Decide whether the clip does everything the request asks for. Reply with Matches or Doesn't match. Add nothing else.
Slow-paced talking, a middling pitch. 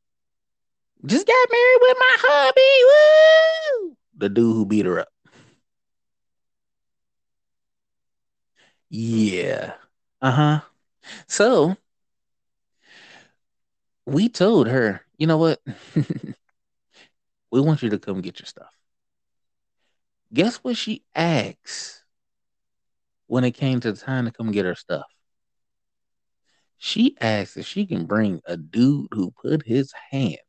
Matches